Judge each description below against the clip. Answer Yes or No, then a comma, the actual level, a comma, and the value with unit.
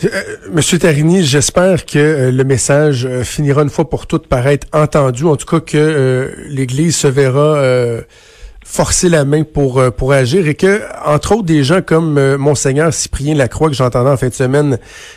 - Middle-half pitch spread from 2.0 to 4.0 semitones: Yes, average, 2.9 semitones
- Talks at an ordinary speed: Yes, average, 190 wpm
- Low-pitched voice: No, medium, 145 Hz